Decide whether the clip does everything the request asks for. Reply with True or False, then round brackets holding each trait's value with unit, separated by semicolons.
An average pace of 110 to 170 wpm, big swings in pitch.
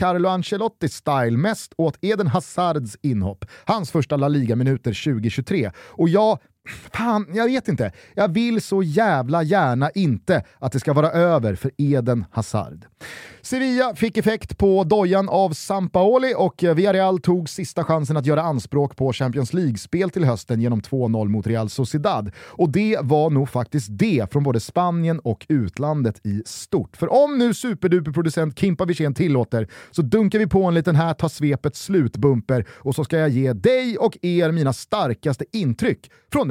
True (160 wpm; 6.4 semitones)